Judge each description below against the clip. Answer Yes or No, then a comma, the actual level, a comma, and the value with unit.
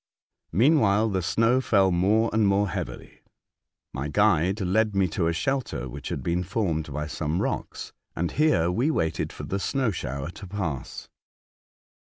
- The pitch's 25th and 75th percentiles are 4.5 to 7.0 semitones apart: Yes, average, 5.2 semitones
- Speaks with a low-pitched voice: Yes, very low, 95 Hz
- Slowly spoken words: No, average, 160 wpm